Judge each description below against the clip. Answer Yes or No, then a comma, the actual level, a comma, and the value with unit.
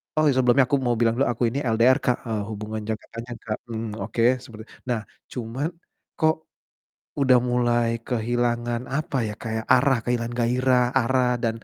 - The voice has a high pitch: No, low, 120 Hz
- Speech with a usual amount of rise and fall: No, narrow, 1.8 semitones